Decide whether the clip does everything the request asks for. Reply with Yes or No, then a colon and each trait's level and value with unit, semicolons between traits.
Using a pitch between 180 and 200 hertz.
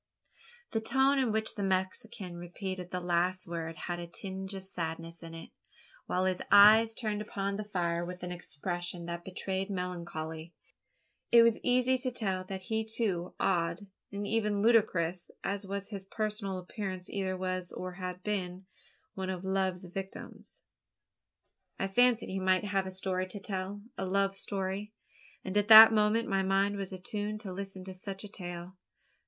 Yes: high, 190 Hz